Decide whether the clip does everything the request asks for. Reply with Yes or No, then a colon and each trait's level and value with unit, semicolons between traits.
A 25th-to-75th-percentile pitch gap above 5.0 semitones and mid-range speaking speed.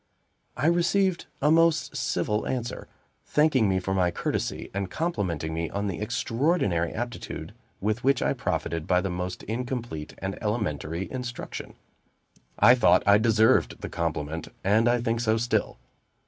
Yes: wide, 5.4 semitones; average, 150 wpm